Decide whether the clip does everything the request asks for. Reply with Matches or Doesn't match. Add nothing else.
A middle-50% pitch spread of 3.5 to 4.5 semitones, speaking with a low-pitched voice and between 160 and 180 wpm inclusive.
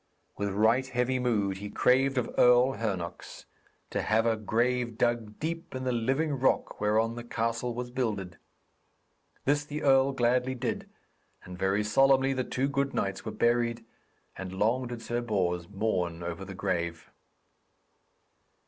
Doesn't match